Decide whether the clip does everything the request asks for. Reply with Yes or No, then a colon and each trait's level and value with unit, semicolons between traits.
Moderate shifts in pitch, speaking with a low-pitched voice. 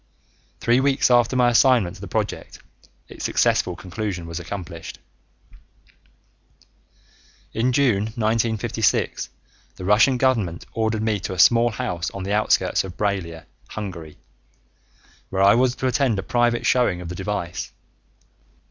Yes: average, 4.7 semitones; low, 105 Hz